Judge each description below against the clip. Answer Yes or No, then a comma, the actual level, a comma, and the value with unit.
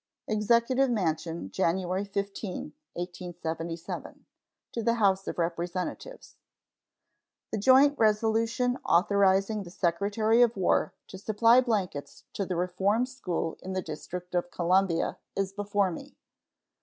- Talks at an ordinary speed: No, slow, 120 wpm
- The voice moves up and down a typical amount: Yes, average, 4.0 semitones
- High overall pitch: Yes, high, 195 Hz